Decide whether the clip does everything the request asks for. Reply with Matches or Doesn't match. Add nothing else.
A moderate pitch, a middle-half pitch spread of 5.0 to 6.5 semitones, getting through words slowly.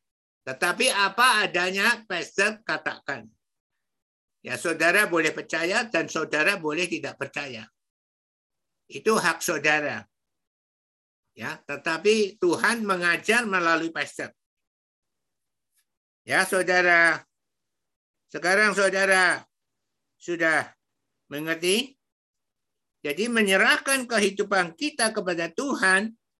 Matches